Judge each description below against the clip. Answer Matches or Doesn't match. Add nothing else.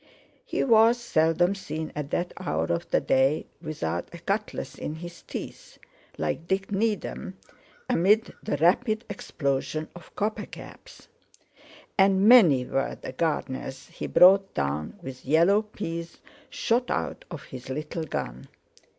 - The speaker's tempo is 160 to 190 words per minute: Doesn't match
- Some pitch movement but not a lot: Doesn't match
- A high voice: Doesn't match